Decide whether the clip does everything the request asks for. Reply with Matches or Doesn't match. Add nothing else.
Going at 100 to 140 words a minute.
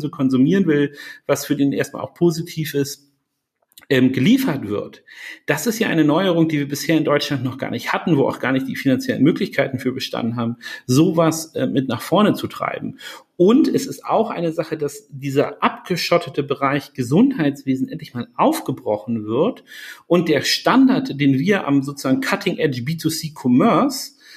Doesn't match